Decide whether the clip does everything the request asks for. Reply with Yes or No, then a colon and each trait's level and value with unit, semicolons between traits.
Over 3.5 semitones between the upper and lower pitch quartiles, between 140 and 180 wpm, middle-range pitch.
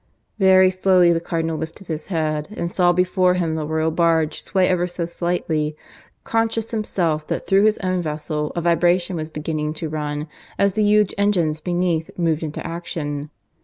No: average, 2.8 semitones; average, 170 wpm; medium, 170 Hz